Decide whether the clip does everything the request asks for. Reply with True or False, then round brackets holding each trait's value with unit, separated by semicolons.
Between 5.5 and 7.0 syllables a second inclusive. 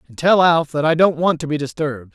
True (6.0 syllables/s)